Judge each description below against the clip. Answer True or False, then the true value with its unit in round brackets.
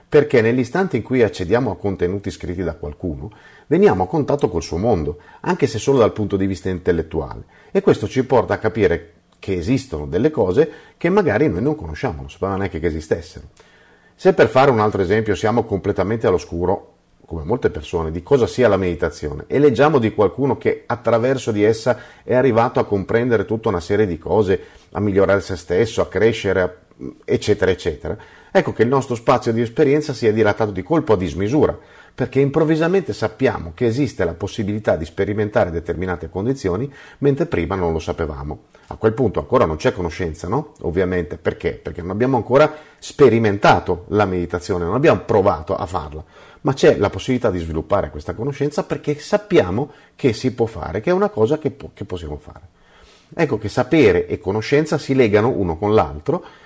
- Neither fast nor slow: False (180 wpm)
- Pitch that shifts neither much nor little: False (6.7 semitones)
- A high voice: False (110 Hz)